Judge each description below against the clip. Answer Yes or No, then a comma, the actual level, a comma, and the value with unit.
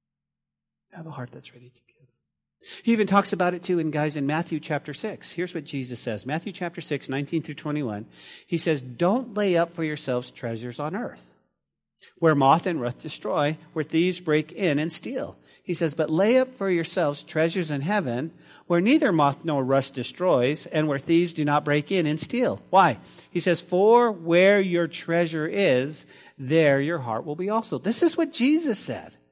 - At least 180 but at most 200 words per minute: Yes, average, 190 wpm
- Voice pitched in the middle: Yes, medium, 160 Hz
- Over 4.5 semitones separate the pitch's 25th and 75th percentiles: No, average, 4.2 semitones